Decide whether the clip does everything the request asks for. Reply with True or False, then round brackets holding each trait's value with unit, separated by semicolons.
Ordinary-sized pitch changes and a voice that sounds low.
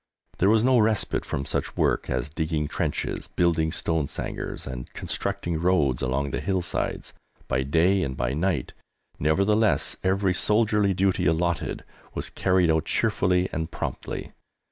True (4.3 semitones; 85 Hz)